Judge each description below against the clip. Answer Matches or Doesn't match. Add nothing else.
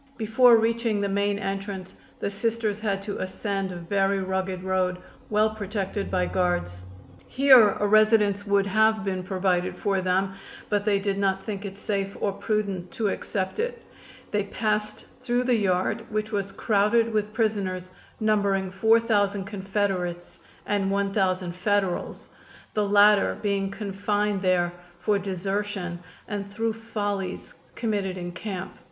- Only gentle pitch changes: Matches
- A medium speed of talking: Matches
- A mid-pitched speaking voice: Doesn't match